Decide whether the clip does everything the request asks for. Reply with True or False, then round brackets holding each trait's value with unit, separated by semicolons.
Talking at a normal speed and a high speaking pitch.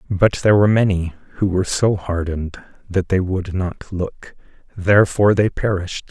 False (155 wpm; 95 Hz)